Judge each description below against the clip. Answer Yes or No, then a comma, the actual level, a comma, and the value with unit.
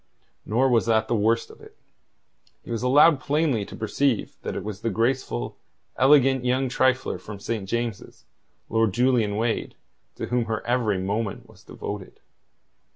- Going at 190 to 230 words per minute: No, average, 155 wpm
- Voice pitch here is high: No, low, 115 Hz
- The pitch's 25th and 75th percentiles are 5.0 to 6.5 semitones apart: No, average, 3.2 semitones